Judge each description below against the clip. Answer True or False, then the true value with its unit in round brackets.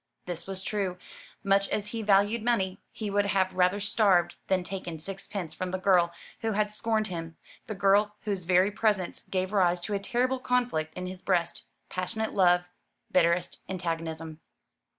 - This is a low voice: False (190 Hz)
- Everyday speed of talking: True (165 wpm)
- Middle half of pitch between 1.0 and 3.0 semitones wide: True (2.6 semitones)